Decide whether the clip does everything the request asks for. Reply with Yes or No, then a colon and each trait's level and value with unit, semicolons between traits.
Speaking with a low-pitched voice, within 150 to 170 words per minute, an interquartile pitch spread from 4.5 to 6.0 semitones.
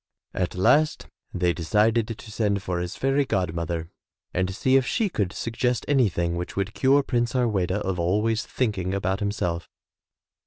Yes: low, 100 Hz; average, 165 wpm; average, 4.9 semitones